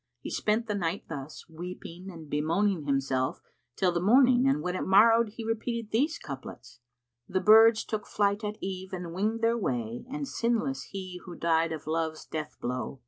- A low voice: No, high, 190 Hz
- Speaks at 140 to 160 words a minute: No, average, 185 wpm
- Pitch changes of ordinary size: No, wide, 5.9 semitones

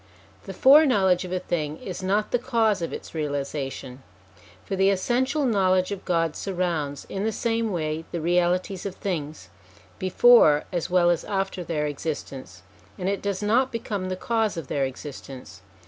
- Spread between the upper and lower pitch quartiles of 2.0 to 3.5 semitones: No, average, 4.7 semitones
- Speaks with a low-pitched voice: No, medium, 185 Hz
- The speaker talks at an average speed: Yes, average, 170 wpm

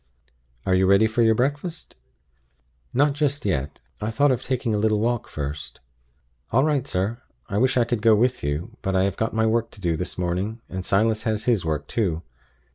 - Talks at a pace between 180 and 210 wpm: Yes, average, 200 wpm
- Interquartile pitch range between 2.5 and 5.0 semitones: Yes, average, 4.6 semitones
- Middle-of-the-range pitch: No, low, 110 Hz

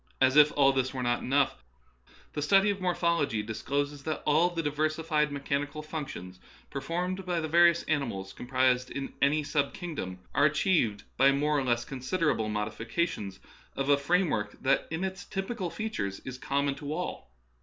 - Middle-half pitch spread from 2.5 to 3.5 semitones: No, average, 4.4 semitones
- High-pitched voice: No, medium, 145 Hz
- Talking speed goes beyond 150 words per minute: Yes, average, 165 wpm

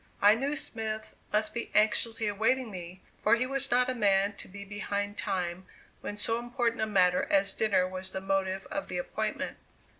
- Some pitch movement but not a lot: Yes, average, 3.2 semitones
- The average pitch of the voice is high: Yes, high, 210 Hz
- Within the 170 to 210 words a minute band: Yes, average, 185 wpm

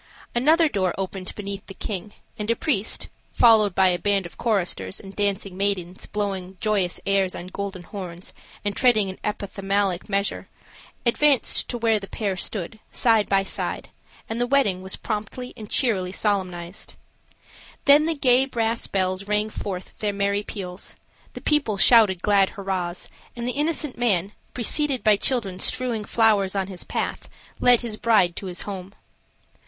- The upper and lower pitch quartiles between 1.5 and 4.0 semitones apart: Yes, average, 3.4 semitones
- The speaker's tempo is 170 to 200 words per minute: No, average, 160 wpm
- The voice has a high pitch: Yes, high, 200 Hz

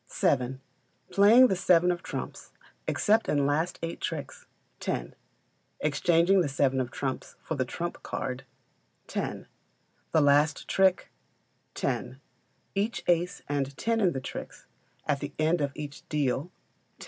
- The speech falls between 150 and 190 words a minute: No, average, 140 wpm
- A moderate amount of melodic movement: Yes, average, 4.2 semitones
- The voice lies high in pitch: No, medium, 155 Hz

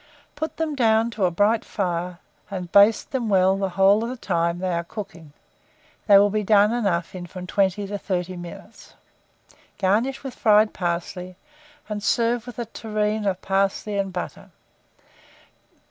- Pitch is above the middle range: Yes, high, 200 Hz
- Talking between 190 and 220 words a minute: No, average, 160 wpm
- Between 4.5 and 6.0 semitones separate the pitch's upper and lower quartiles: No, average, 3.2 semitones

